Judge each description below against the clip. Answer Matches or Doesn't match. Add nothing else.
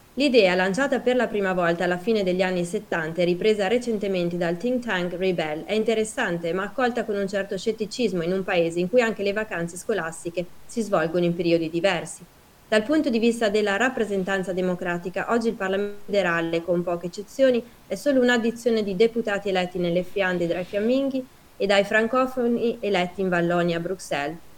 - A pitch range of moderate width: Matches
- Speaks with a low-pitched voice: Doesn't match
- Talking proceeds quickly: Matches